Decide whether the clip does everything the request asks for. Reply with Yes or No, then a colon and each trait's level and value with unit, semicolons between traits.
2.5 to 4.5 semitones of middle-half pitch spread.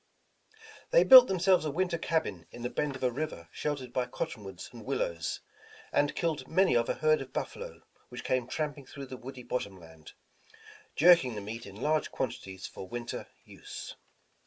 No: wide, 5.4 semitones